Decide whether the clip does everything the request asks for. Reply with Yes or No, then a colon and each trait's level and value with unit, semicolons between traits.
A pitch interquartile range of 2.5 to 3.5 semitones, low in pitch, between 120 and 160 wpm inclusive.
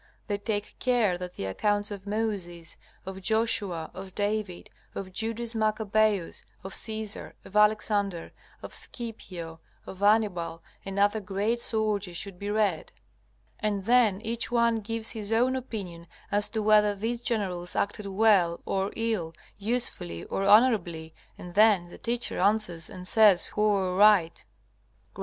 No: average, 3.0 semitones; high, 205 Hz; average, 145 wpm